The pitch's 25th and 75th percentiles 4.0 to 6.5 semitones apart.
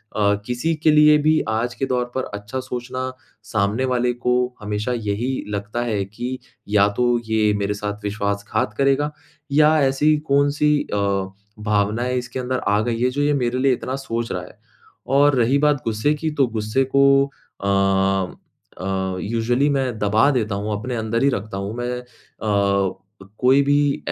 Yes: average, 4.3 semitones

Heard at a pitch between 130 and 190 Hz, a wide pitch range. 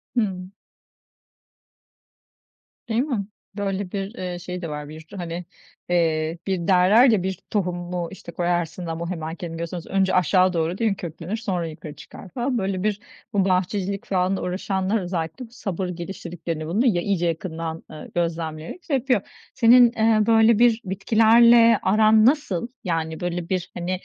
No: medium, 185 Hz; average, 3.9 semitones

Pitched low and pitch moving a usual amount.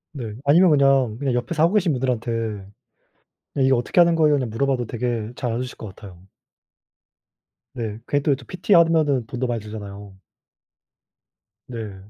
Yes: low, 125 Hz; average, 4.4 semitones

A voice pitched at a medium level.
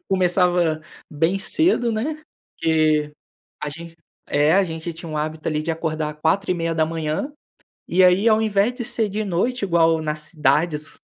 Yes: medium, 165 Hz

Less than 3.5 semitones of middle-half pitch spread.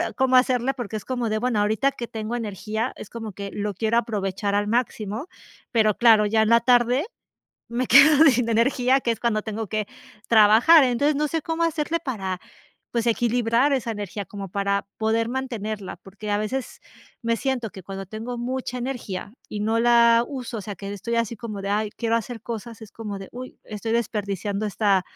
Yes: average, 3.0 semitones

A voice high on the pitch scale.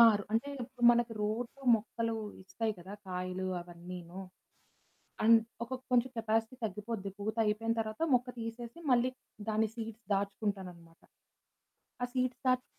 Yes: high, 225 Hz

